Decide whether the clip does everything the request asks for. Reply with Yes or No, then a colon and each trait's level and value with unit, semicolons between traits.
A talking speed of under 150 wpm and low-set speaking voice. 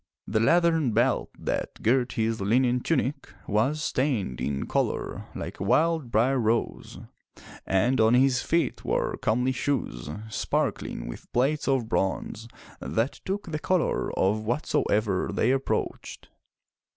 Yes: slow, 135 wpm; low, 125 Hz